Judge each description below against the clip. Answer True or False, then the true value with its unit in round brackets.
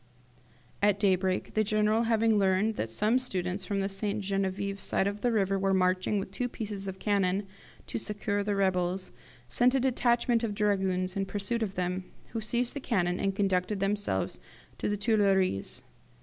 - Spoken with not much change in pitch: True (2.1 semitones)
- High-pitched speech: True (200 Hz)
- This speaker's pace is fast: False (175 wpm)